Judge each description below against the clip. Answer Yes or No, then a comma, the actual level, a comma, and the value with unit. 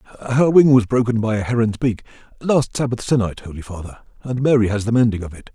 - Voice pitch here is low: Yes, low, 115 Hz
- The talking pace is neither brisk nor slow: No, fast, 215 wpm